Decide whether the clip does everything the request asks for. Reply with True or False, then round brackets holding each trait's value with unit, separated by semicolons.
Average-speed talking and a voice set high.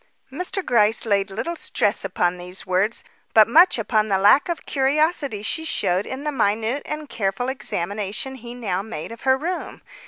True (175 wpm; 225 Hz)